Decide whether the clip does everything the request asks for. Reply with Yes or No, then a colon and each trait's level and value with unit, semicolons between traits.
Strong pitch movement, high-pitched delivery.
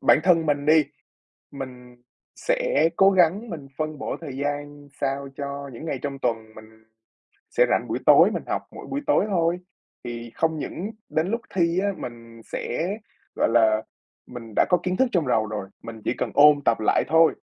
No: wide, 5.9 semitones; medium, 145 Hz